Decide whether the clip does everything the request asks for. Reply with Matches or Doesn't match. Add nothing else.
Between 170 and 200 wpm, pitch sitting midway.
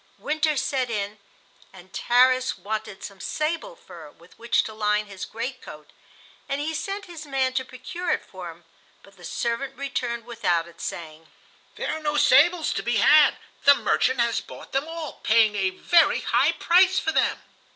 Doesn't match